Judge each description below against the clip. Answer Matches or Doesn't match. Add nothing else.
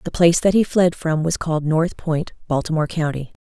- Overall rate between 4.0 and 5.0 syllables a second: Doesn't match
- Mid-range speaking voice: Matches